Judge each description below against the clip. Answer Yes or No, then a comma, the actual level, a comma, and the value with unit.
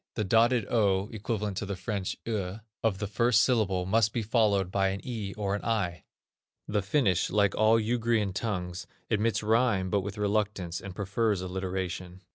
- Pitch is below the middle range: Yes, low, 100 Hz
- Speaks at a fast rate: No, average, 170 wpm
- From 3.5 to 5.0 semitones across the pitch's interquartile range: No, average, 2.8 semitones